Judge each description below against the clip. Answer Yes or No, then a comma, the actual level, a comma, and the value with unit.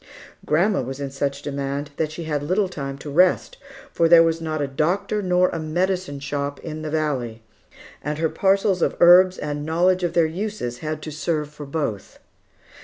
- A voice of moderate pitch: Yes, medium, 155 Hz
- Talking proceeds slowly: No, average, 185 wpm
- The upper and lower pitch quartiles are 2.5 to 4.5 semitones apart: Yes, average, 3.7 semitones